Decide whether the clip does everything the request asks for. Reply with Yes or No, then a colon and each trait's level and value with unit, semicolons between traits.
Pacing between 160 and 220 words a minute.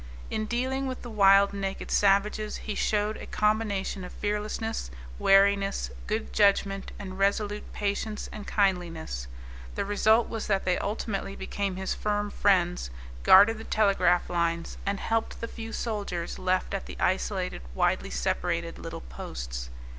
No: average, 145 wpm